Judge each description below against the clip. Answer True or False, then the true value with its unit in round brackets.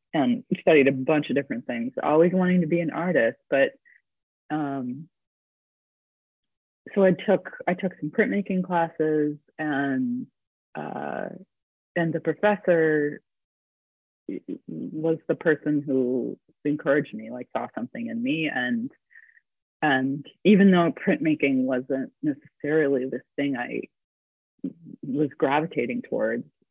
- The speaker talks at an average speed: False (115 wpm)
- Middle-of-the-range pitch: True (160 Hz)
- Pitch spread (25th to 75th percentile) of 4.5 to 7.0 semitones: True (5.3 semitones)